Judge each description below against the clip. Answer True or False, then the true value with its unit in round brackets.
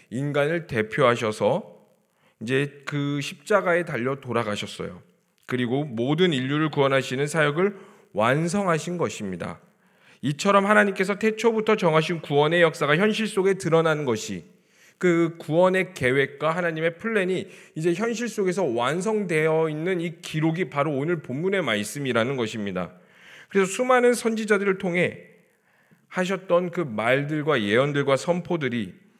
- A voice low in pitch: False (165 Hz)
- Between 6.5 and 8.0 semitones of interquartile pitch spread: False (5.3 semitones)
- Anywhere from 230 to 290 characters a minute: False (310 characters per minute)